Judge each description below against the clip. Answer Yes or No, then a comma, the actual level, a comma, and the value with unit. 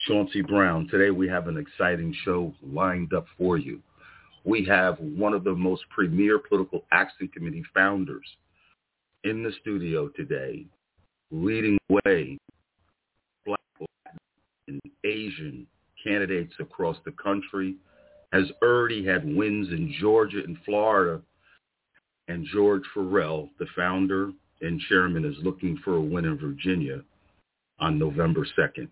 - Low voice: Yes, low, 100 Hz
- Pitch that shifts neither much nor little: No, wide, 7.1 semitones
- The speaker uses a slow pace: Yes, slow, 130 wpm